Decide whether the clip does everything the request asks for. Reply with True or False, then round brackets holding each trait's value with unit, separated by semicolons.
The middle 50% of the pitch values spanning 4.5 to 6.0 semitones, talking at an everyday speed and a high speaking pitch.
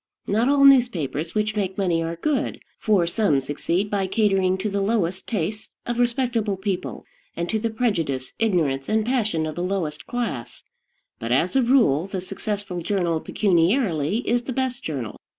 True (5.2 semitones; 170 wpm; 200 Hz)